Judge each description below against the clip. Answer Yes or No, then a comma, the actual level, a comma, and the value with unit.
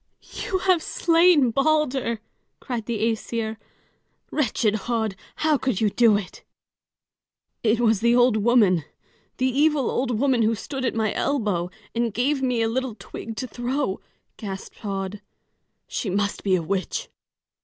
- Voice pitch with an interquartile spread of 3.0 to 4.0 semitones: Yes, average, 3.7 semitones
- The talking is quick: No, average, 145 wpm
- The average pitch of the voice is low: No, high, 235 Hz